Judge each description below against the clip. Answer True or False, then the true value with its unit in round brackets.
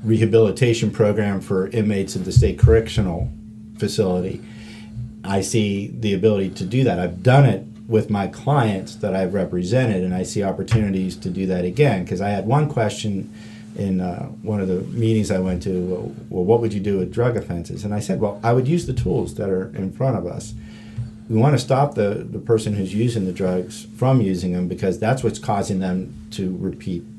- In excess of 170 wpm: True (205 wpm)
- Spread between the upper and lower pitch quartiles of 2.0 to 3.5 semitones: True (3.0 semitones)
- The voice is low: True (105 Hz)